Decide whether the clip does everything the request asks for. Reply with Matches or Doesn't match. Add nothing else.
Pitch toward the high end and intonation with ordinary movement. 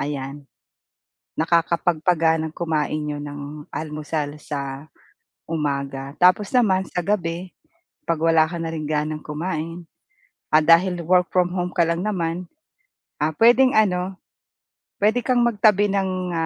Doesn't match